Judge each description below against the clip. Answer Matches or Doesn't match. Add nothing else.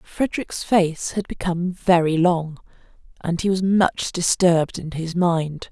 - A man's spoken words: Doesn't match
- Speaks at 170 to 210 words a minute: Doesn't match